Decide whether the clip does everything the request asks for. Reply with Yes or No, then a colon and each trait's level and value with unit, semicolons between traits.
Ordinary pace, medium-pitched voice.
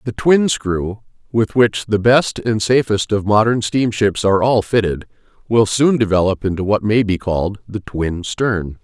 No: average, 185 wpm; low, 110 Hz